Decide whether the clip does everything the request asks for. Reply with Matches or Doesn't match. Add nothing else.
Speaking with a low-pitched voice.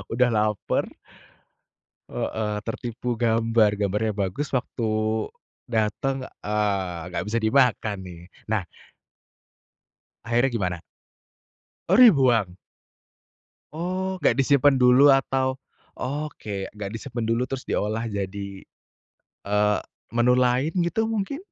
Matches